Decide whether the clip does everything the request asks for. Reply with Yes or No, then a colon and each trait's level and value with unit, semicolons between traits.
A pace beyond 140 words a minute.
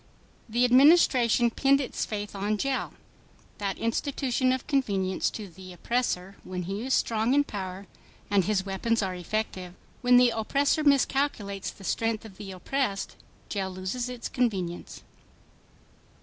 No: slow, 135 wpm